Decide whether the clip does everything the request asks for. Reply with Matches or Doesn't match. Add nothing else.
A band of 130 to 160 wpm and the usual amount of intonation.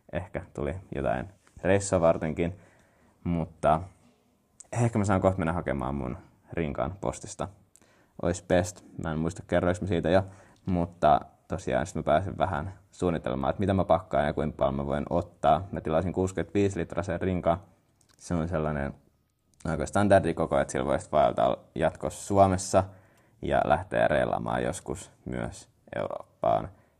Matches